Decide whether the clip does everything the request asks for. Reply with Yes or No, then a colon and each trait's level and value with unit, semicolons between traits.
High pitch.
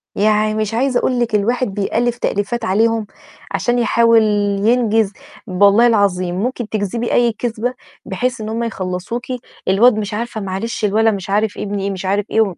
Yes: high, 220 Hz